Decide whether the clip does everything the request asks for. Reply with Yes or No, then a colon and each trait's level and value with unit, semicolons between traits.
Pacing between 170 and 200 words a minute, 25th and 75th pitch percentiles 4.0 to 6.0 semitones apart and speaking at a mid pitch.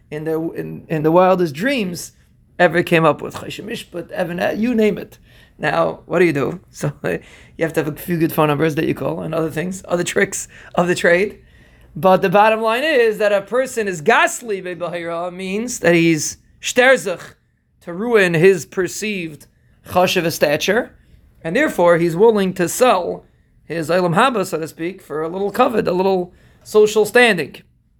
Yes: average, 180 wpm; average, 4.5 semitones; medium, 175 Hz